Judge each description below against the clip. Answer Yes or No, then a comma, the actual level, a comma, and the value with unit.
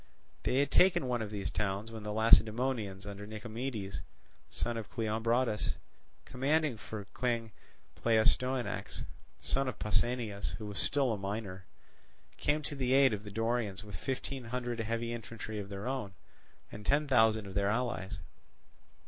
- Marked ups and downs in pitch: No, average, 3.4 semitones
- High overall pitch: No, low, 115 Hz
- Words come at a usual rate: Yes, average, 150 wpm